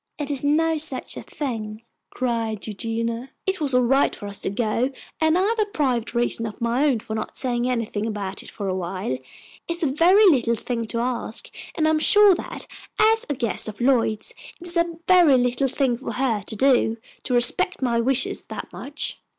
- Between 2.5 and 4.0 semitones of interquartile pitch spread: No, average, 5.0 semitones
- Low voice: No, very high, 250 Hz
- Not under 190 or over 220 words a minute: Yes, average, 200 wpm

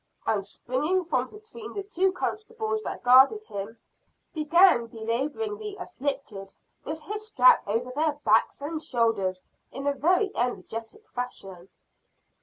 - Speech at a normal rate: No, slow, 130 wpm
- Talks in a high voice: Yes, very high, 290 Hz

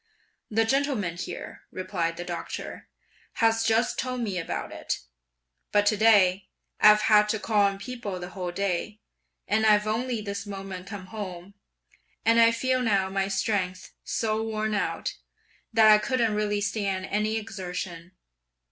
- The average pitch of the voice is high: Yes, high, 210 Hz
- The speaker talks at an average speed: Yes, average, 150 wpm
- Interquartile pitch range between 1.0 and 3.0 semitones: Yes, average, 2.7 semitones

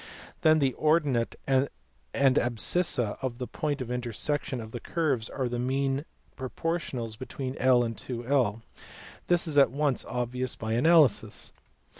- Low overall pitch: Yes, low, 130 Hz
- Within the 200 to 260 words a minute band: No, average, 145 wpm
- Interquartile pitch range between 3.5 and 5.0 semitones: No, average, 3.1 semitones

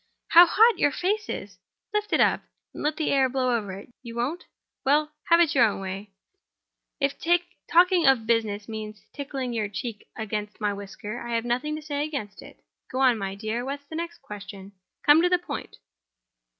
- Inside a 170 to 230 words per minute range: Yes, average, 180 wpm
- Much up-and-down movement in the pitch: Yes, wide, 6.2 semitones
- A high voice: Yes, very high, 255 Hz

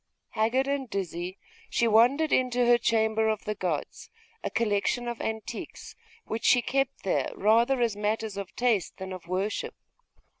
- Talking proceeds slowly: No, average, 155 wpm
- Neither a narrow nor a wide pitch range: Yes, average, 3.2 semitones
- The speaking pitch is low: No, high, 220 Hz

